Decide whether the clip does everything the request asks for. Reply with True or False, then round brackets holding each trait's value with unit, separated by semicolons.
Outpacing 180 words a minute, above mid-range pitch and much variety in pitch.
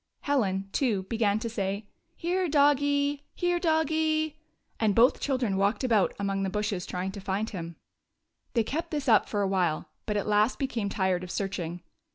True (190 wpm; 215 Hz; 6.6 semitones)